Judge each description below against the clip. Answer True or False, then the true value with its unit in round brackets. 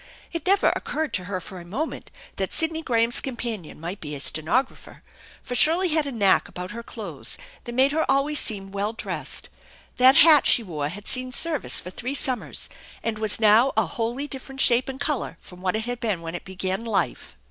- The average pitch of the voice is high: True (235 Hz)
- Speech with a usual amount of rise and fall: False (6.0 semitones)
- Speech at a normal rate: False (210 wpm)